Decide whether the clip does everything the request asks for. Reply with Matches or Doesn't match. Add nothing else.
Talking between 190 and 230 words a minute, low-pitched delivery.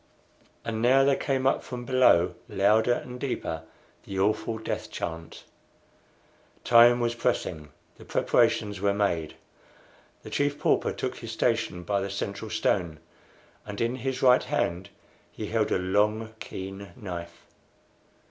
Doesn't match